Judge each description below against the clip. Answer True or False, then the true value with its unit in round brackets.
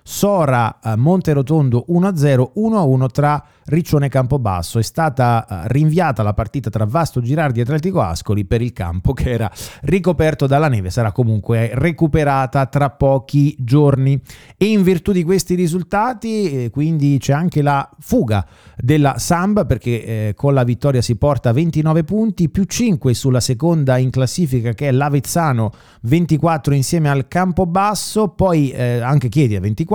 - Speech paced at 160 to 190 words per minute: False (150 wpm)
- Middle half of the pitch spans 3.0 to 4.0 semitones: False (5.3 semitones)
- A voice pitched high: False (140 Hz)